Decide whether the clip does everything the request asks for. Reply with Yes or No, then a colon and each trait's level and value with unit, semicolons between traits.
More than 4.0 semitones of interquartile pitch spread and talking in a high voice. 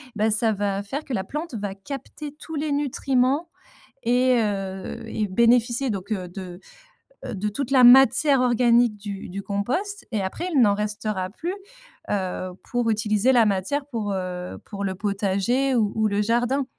Yes: average, 4.5 semitones; high, 220 Hz